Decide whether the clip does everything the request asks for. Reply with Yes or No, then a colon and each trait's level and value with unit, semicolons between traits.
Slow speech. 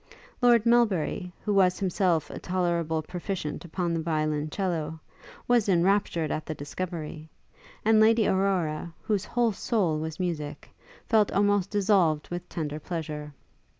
Yes: slow, 130 wpm